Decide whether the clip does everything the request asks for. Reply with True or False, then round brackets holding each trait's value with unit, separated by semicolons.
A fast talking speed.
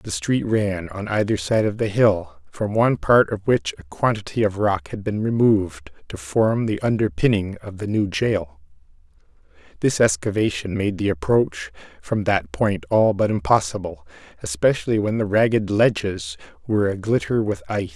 False (165 wpm)